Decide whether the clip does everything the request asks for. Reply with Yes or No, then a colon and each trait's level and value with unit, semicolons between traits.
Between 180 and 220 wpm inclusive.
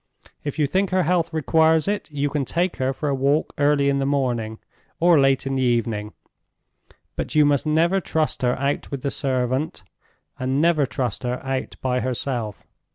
Yes: average, 185 wpm